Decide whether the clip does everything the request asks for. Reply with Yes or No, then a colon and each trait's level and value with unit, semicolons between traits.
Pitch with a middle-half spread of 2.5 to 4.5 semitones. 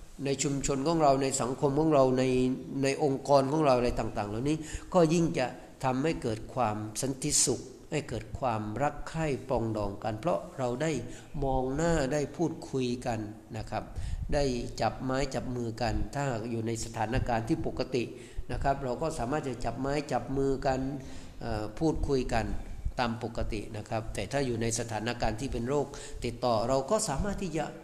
Yes: average, 3.8 semitones